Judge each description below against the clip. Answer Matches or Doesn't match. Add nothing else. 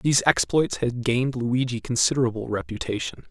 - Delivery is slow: Matches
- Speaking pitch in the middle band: Doesn't match